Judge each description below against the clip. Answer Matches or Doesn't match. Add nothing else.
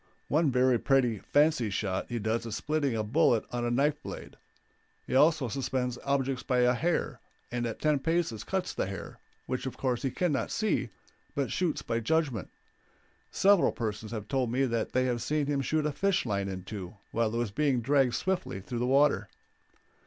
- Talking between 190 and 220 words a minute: Matches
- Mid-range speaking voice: Doesn't match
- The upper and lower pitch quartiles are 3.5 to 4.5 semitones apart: Matches